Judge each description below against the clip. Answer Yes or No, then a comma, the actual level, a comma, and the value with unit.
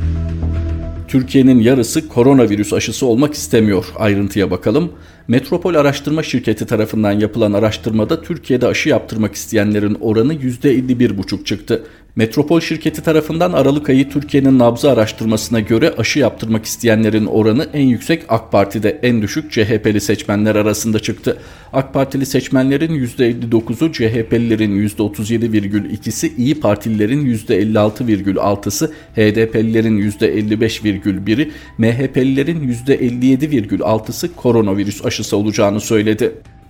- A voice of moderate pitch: No, low, 115 Hz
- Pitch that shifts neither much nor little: Yes, average, 4.0 semitones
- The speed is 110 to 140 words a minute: No, average, 100 wpm